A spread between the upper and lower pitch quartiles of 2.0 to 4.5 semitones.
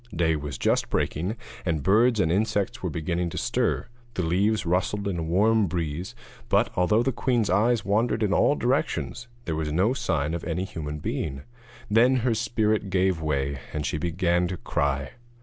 No: average, 5.2 semitones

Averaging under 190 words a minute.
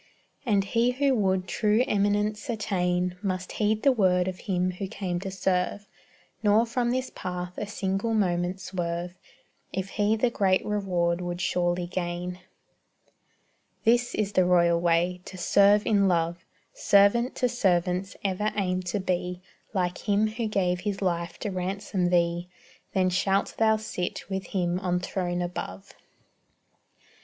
Yes: average, 150 wpm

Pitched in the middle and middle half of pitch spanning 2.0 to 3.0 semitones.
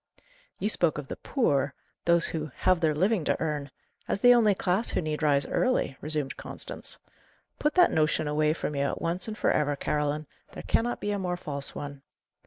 No: medium, 155 Hz; average, 5.0 semitones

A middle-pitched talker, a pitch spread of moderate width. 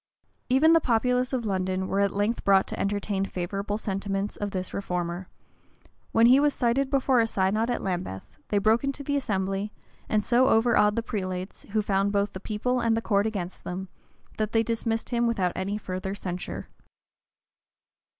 No: high, 205 Hz; average, 3.4 semitones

